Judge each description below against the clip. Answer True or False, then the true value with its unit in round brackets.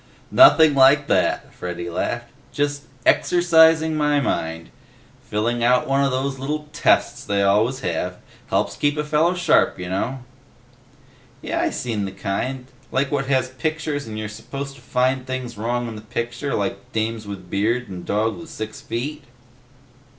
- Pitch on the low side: True (125 Hz)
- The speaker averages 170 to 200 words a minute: False (160 wpm)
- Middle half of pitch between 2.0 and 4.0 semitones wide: False (5.1 semitones)